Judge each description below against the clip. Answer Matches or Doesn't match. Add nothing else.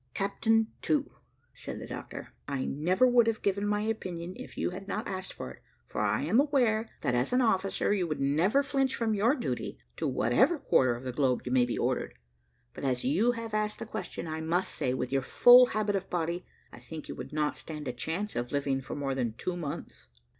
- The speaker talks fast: Matches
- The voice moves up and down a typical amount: Doesn't match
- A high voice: Doesn't match